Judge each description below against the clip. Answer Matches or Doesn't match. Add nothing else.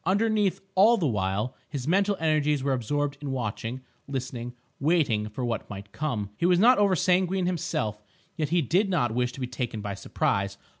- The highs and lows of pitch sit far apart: Matches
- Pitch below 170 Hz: Matches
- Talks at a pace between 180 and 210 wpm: Matches